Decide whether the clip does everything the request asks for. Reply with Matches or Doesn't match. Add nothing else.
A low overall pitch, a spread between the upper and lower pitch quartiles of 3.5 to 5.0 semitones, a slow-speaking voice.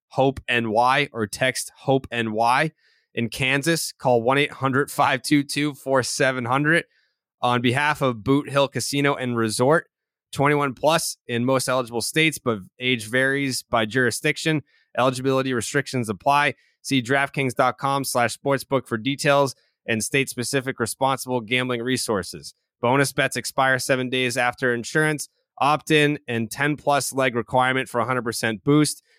Doesn't match